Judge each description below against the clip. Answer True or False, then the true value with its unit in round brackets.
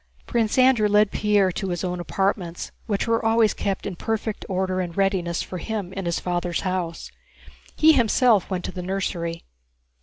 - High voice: True (195 Hz)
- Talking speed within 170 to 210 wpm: True (175 wpm)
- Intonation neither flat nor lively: True (3.2 semitones)